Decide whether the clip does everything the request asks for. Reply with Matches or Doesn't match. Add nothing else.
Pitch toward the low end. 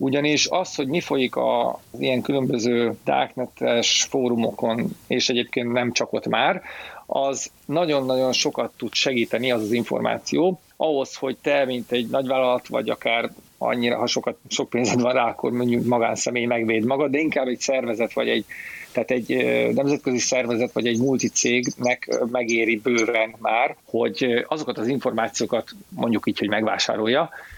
Matches